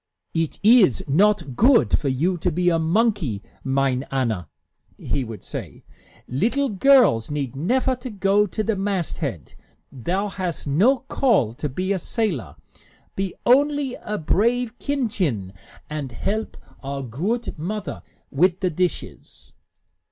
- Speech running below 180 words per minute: Yes, slow, 135 wpm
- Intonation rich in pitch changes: Yes, wide, 8.1 semitones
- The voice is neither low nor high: Yes, medium, 180 Hz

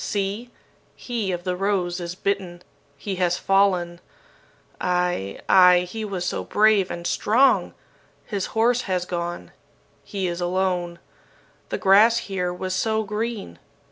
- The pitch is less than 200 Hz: Yes, medium, 185 Hz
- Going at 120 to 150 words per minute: Yes, slow, 135 wpm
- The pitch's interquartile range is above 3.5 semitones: No, average, 2.8 semitones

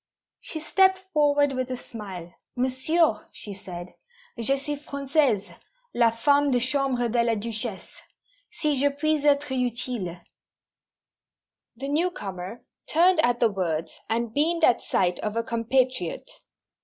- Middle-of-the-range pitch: No, very high, 250 Hz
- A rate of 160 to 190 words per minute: No, slow, 135 wpm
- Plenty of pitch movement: No, average, 4.7 semitones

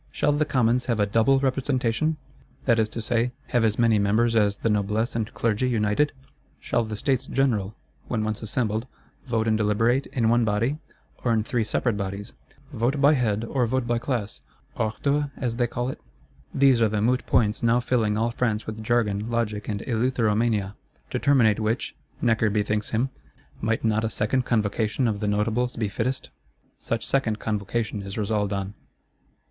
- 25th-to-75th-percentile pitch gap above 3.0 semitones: No, narrow, 2.6 semitones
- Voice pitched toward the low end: Yes, low, 115 Hz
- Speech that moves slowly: No, average, 175 wpm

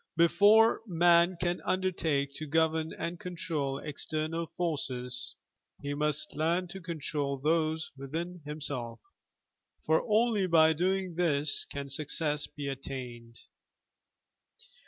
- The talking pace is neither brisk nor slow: No, slow, 110 wpm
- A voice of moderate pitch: Yes, medium, 160 Hz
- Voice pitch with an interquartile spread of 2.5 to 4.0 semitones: Yes, average, 3.5 semitones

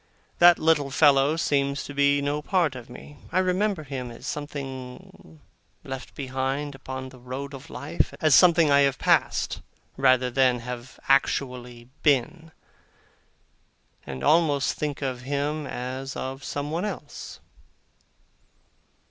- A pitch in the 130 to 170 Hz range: Yes, medium, 140 Hz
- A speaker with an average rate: No, slow, 130 wpm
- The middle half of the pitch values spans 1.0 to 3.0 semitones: Yes, narrow, 2.5 semitones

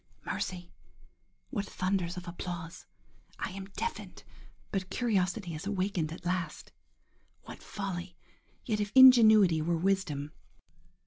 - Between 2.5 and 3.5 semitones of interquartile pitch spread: Yes, average, 2.8 semitones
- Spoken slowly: Yes, slow, 100 wpm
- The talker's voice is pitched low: No, medium, 185 Hz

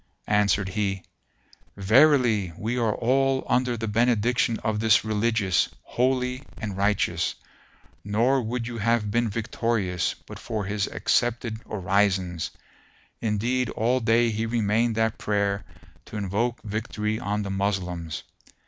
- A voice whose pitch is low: Yes, low, 110 Hz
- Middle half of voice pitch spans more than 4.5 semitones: No, average, 2.7 semitones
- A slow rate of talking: Yes, slow, 125 wpm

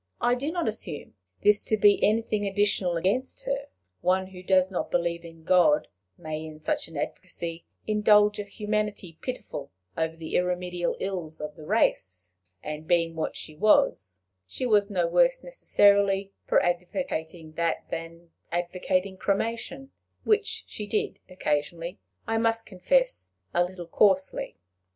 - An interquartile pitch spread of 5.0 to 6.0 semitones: No, average, 4.2 semitones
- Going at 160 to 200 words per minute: No, average, 145 wpm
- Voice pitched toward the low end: No, medium, 185 Hz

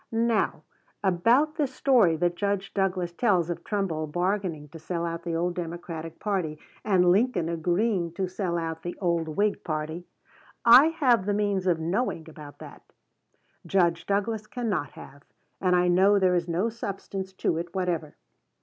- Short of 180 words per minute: Yes, average, 160 wpm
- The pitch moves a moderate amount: Yes, average, 3.4 semitones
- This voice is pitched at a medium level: Yes, medium, 180 Hz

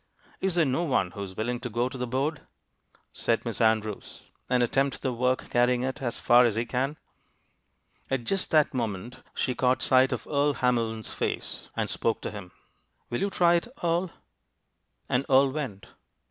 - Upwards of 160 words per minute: Yes, average, 180 wpm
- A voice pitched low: Yes, low, 125 Hz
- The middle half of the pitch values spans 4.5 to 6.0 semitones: No, average, 3.0 semitones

